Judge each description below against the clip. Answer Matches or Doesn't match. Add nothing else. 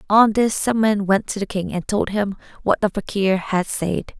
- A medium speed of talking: Doesn't match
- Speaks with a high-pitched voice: Matches